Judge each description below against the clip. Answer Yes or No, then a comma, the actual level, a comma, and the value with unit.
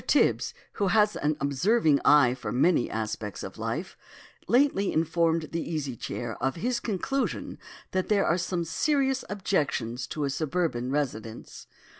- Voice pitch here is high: No, medium, 160 Hz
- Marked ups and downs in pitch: Yes, wide, 6.8 semitones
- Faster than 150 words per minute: No, average, 145 wpm